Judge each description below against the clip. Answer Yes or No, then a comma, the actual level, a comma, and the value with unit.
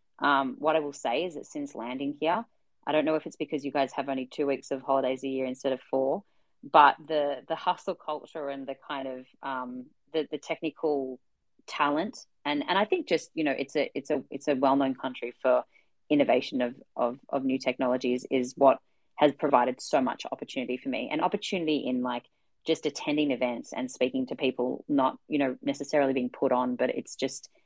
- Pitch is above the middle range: No, medium, 140 Hz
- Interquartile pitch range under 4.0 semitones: Yes, average, 3.1 semitones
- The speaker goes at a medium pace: No, fast, 210 wpm